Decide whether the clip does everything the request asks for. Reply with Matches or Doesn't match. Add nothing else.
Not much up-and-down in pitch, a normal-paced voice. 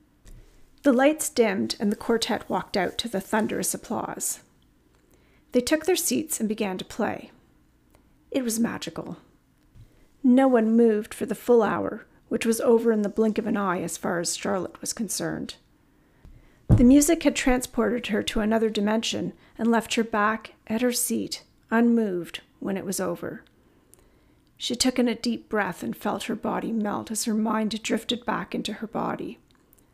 Matches